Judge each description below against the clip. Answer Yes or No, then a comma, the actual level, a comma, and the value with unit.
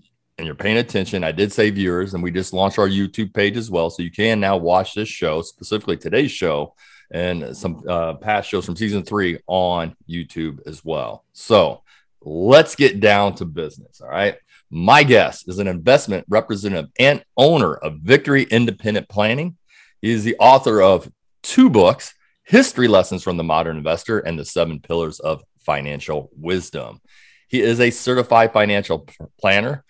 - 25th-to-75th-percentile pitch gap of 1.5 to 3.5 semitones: No, average, 4.2 semitones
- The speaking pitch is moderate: No, very low, 95 Hz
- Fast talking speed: No, average, 170 wpm